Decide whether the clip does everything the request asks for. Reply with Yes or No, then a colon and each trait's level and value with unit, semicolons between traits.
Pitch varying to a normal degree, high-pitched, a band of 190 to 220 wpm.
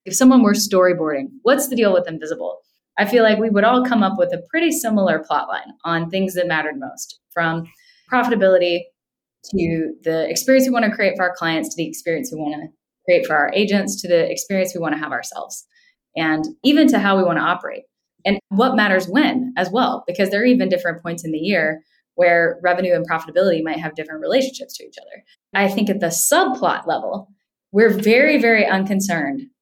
No: wide, 6.7 semitones; high, 195 Hz; average, 200 wpm